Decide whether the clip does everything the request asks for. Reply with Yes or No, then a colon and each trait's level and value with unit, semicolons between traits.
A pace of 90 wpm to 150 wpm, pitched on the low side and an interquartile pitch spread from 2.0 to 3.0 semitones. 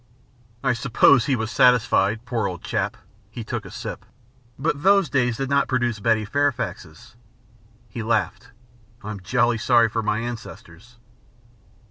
Yes: average, 140 wpm; low, 120 Hz; narrow, 2.6 semitones